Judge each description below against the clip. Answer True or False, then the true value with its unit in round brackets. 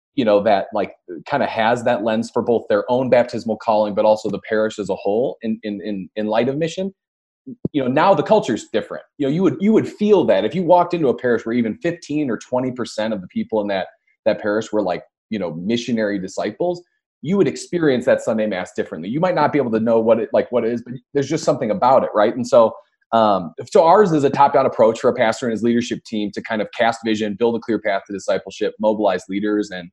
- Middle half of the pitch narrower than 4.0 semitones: False (5.0 semitones)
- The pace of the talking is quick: True (250 wpm)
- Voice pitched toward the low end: True (115 Hz)